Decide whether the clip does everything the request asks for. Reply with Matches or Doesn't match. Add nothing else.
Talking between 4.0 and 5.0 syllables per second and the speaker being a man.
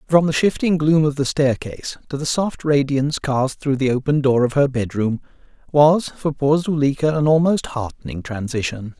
Matches